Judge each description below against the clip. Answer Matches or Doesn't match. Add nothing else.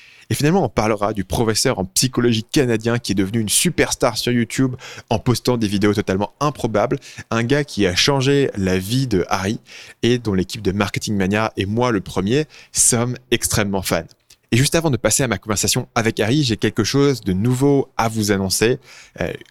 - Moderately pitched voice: Doesn't match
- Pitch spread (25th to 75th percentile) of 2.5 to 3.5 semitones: Doesn't match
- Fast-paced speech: Doesn't match